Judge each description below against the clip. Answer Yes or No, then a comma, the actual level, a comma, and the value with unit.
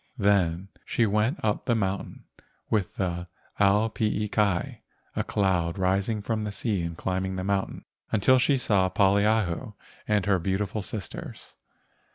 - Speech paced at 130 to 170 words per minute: Yes, average, 150 wpm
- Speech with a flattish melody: Yes, narrow, 2.2 semitones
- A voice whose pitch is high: No, low, 100 Hz